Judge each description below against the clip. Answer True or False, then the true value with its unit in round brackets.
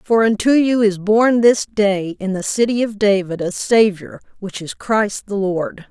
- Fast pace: False (195 wpm)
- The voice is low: False (210 Hz)